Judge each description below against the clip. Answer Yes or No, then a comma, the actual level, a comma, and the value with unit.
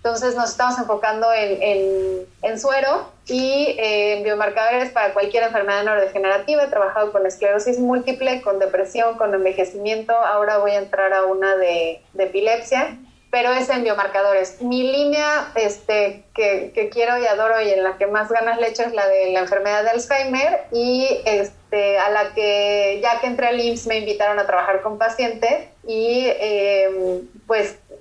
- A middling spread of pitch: Yes, average, 3.2 semitones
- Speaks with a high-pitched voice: Yes, high, 215 Hz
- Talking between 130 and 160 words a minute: No, average, 170 wpm